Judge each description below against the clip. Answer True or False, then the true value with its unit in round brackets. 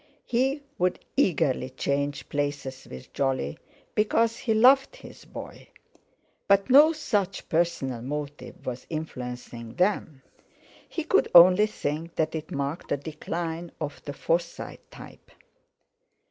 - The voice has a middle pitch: True (160 Hz)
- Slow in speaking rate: True (120 wpm)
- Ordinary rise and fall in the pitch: False (6.6 semitones)